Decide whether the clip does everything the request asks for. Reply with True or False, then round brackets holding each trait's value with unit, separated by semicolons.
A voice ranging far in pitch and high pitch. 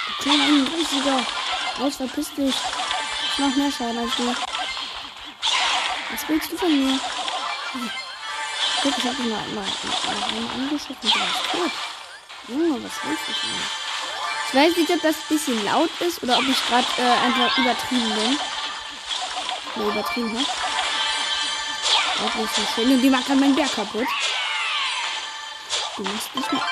False (3.0 semitones; 265 Hz)